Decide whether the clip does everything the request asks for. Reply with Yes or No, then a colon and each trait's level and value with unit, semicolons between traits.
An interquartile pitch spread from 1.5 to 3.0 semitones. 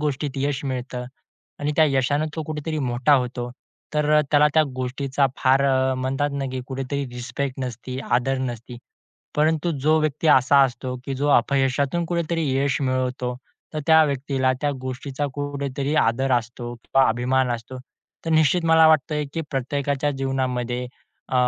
Yes: narrow, 2.4 semitones